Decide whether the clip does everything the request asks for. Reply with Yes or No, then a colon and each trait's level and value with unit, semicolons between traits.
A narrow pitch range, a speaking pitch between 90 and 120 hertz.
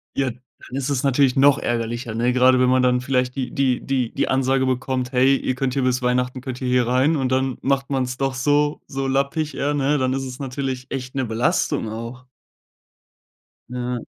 No: narrow, 1.3 semitones; low, 130 Hz